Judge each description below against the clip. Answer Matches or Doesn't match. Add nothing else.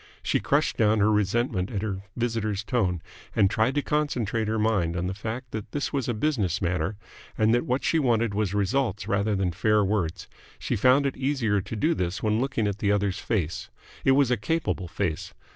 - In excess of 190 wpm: Matches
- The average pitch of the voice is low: Matches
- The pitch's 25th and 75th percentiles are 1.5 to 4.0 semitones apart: Matches